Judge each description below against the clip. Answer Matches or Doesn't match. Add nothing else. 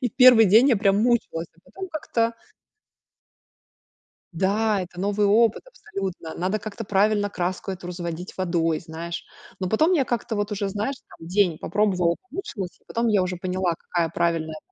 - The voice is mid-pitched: Doesn't match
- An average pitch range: Matches